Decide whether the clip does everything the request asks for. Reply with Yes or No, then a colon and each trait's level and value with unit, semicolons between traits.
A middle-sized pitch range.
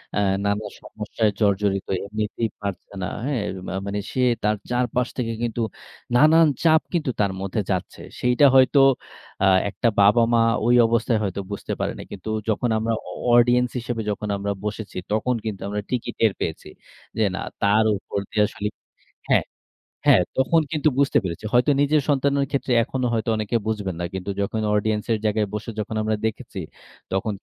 Yes: average, 3.2 semitones